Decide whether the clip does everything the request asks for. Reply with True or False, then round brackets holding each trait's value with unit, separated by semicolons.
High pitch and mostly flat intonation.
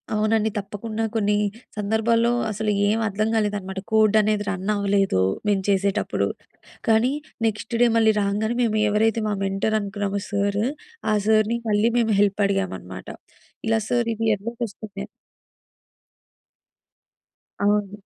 True (210 Hz; 1.7 semitones)